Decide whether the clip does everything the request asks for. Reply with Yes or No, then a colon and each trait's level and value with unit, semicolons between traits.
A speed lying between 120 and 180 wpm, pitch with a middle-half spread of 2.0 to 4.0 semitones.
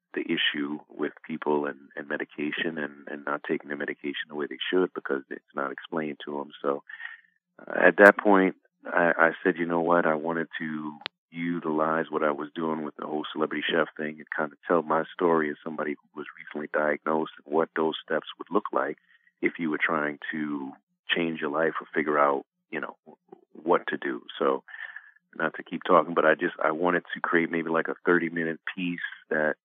No: average, 200 wpm; narrow, 2.5 semitones